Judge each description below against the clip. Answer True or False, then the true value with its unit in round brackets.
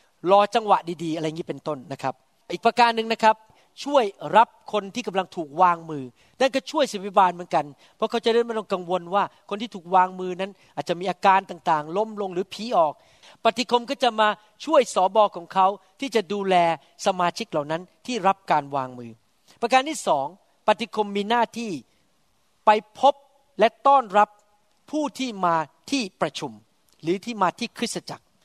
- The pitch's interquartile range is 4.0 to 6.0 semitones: True (4.7 semitones)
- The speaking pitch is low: False (200 Hz)